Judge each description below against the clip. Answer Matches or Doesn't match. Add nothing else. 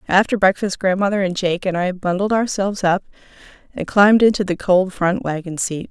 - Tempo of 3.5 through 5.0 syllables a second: Doesn't match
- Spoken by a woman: Matches